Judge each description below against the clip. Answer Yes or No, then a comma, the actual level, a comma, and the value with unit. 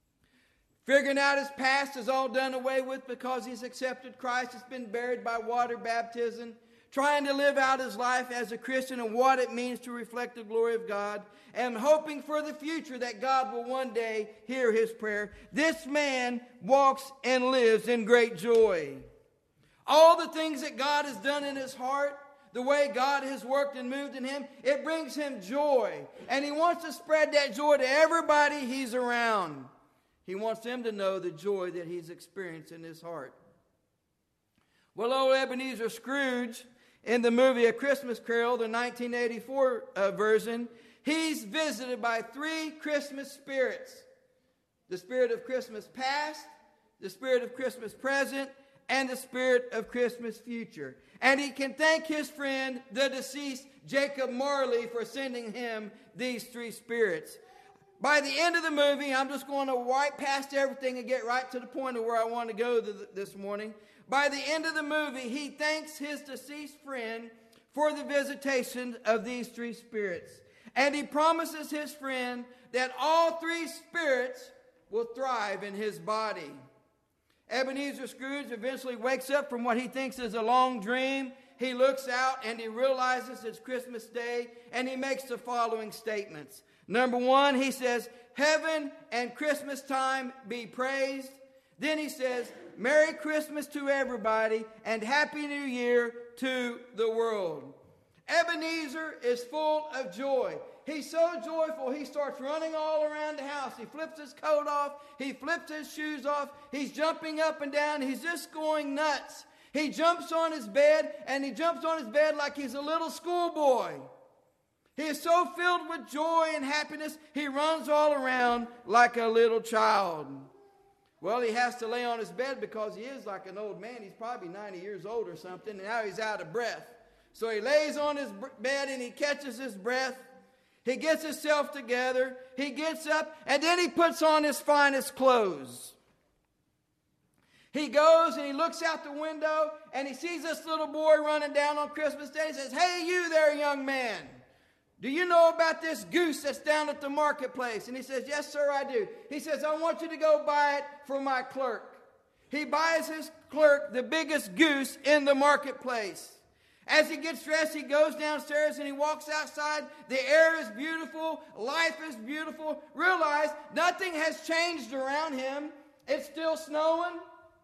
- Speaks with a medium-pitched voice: No, very high, 270 Hz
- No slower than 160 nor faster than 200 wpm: Yes, average, 175 wpm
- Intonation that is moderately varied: Yes, average, 3.8 semitones